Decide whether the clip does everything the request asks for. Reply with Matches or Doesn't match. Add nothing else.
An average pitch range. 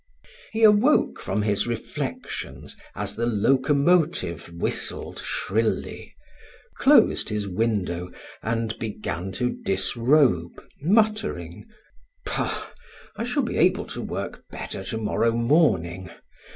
Doesn't match